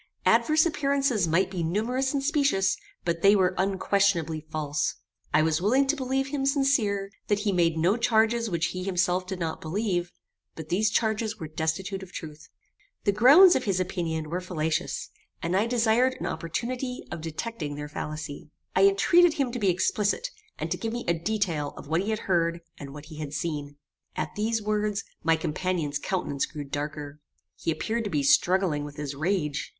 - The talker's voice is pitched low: No, medium, 185 Hz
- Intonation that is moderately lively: No, wide, 5.8 semitones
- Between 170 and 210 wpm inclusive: Yes, average, 185 wpm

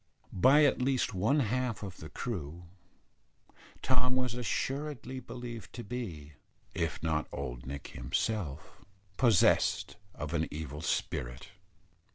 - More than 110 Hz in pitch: No, low, 100 Hz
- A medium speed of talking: No, slow, 120 wpm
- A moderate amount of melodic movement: No, wide, 8.6 semitones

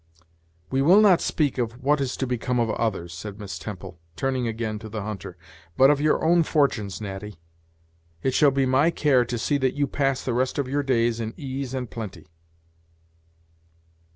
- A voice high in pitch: No, low, 125 Hz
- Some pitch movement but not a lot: Yes, average, 4.1 semitones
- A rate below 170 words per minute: No, average, 185 wpm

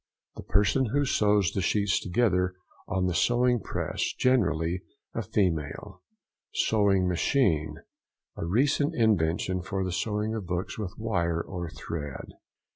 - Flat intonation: No, average, 4.1 semitones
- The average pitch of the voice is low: Yes, very low, 95 Hz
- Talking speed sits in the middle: No, slow, 120 wpm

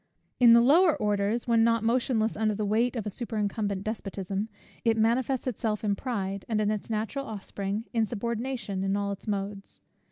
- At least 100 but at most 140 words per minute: No, average, 165 wpm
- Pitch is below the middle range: No, high, 220 Hz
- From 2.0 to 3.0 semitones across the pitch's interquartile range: Yes, narrow, 2.6 semitones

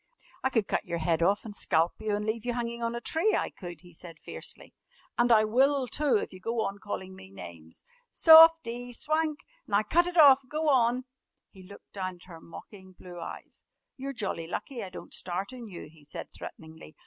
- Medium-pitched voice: No, high, 215 Hz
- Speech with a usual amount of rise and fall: No, wide, 6.2 semitones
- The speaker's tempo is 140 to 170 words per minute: No, fast, 205 wpm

